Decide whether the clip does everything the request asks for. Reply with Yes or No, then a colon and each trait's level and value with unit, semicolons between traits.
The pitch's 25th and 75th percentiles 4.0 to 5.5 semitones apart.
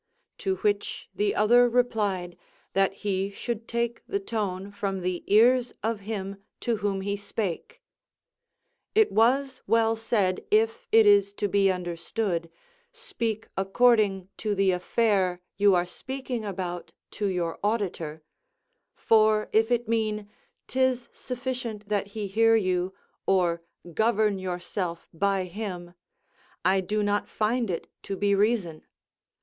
No: average, 3.0 semitones